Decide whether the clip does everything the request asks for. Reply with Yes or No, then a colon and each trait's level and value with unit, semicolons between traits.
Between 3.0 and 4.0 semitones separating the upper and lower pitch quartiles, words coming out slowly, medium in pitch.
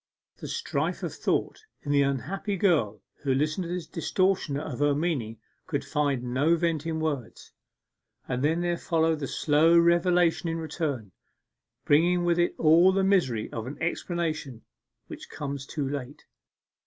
No: average, 3.6 semitones; average, 155 wpm; medium, 155 Hz